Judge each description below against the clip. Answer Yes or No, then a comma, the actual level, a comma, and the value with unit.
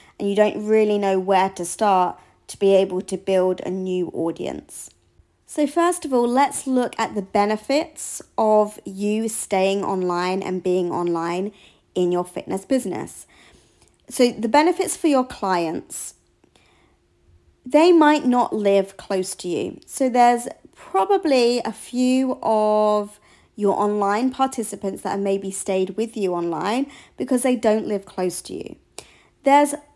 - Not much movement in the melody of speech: No, average, 5.2 semitones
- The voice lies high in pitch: Yes, high, 210 Hz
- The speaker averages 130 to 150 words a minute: Yes, average, 145 wpm